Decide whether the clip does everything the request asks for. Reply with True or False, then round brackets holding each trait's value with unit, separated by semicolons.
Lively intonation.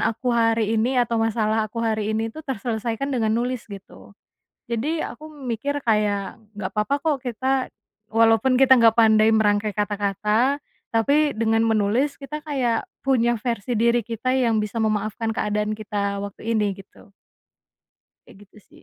False (2.9 semitones)